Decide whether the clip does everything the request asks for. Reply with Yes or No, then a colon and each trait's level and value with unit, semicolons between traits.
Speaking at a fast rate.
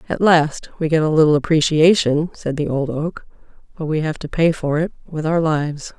Yes: fast, 210 wpm